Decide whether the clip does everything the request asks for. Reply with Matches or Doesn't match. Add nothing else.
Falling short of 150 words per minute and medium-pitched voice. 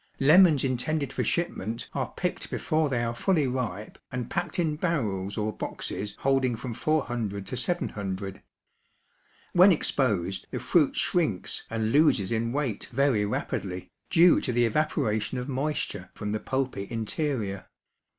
Doesn't match